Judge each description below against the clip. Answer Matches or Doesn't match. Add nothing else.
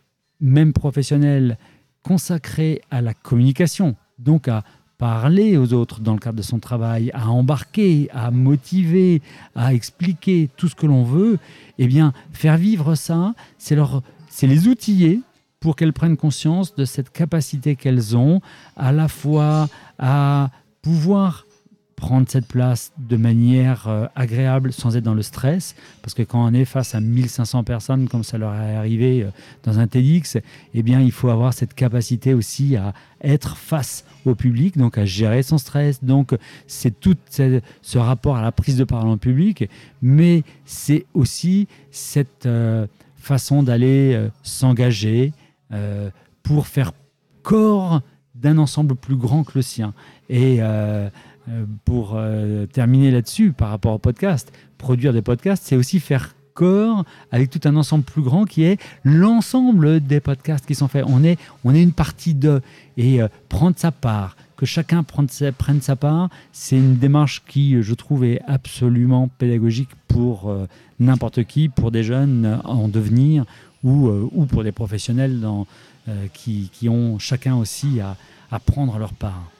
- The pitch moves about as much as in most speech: Matches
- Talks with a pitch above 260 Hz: Doesn't match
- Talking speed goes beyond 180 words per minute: Doesn't match